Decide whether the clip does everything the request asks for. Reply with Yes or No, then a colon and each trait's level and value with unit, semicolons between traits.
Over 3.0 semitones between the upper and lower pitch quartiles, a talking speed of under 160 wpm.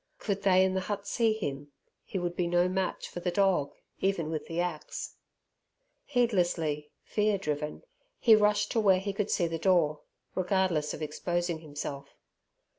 No: average, 3.9 semitones; average, 165 wpm